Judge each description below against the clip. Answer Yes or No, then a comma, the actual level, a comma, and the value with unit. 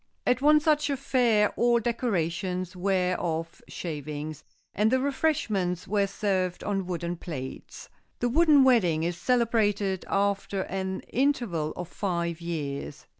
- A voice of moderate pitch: No, high, 195 Hz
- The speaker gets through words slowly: Yes, slow, 125 wpm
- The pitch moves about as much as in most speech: No, wide, 5.7 semitones